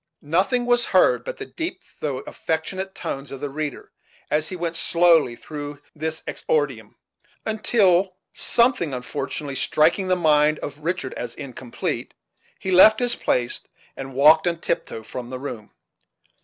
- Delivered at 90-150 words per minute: Yes, average, 145 wpm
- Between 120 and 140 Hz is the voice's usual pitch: No, medium, 155 Hz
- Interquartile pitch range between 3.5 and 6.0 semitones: Yes, average, 5.1 semitones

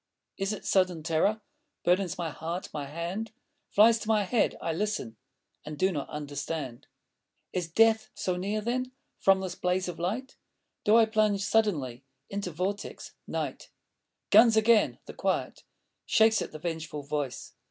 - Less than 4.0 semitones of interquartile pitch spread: No, average, 5.1 semitones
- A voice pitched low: No, medium, 185 Hz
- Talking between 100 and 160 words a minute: Yes, average, 150 wpm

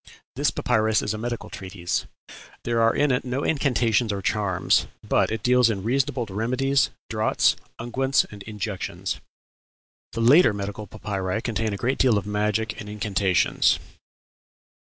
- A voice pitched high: No, low, 110 Hz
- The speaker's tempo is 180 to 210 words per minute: No, average, 145 wpm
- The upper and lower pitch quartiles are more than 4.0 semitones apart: No, average, 3.2 semitones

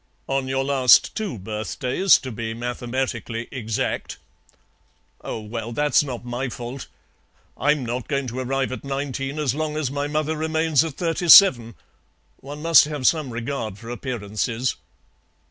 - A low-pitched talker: Yes, low, 130 Hz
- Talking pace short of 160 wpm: Yes, average, 145 wpm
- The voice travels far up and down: No, average, 3.7 semitones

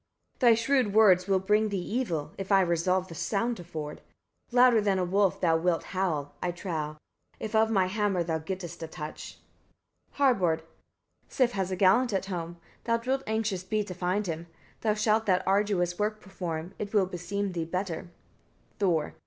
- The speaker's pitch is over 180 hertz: Yes, high, 190 Hz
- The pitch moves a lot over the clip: No, average, 3.5 semitones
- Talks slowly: No, average, 180 wpm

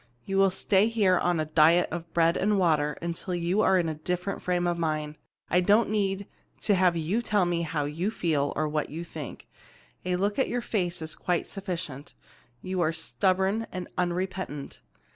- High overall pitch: No, medium, 175 Hz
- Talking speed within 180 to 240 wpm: Yes, average, 190 wpm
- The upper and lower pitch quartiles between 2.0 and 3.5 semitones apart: Yes, average, 3.0 semitones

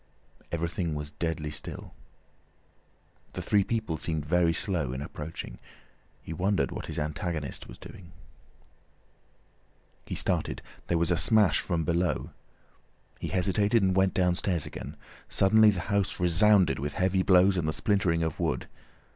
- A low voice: Yes, very low, 85 Hz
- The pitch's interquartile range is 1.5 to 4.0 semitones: Yes, average, 3.4 semitones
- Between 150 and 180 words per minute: No, average, 140 wpm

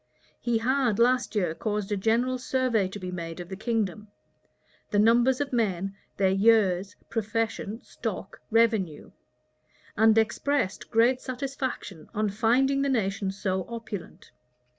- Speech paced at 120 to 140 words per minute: Yes, slow, 135 wpm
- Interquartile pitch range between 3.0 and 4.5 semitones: Yes, average, 3.7 semitones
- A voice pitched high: Yes, high, 220 Hz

